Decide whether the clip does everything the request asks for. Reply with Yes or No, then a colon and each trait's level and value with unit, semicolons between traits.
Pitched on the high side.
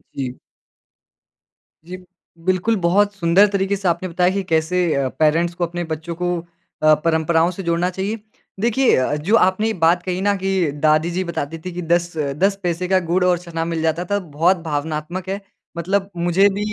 No: medium, 175 Hz